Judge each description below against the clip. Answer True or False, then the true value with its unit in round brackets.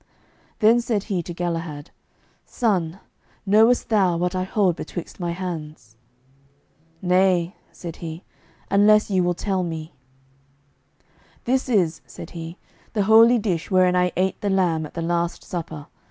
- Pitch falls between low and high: True (180 Hz)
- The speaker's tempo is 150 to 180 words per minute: False (140 wpm)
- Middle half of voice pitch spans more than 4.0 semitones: False (3.2 semitones)